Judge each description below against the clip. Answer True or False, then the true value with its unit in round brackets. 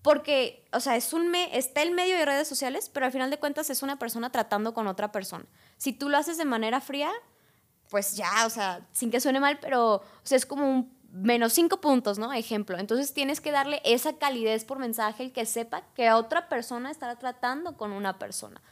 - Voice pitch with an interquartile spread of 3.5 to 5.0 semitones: True (4.1 semitones)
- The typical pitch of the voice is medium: False (255 Hz)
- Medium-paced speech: False (220 wpm)